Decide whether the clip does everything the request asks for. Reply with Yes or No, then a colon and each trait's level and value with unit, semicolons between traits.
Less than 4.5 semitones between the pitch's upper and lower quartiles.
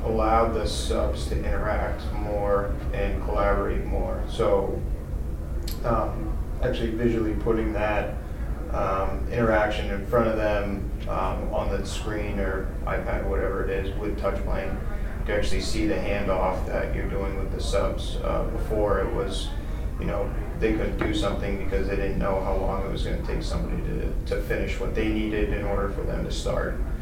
Yes: average, 3.5 semitones